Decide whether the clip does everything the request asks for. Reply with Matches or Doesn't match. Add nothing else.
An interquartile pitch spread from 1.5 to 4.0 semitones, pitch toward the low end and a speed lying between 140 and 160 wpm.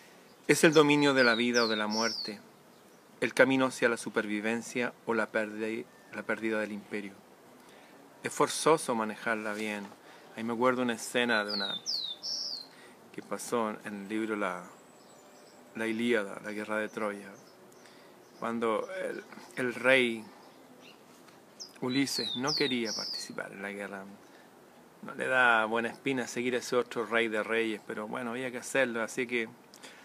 Matches